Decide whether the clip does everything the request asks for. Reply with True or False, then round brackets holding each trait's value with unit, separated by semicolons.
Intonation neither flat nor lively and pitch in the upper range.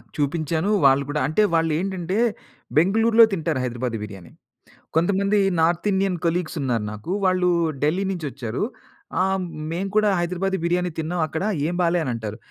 False (4.7 semitones; 170 Hz)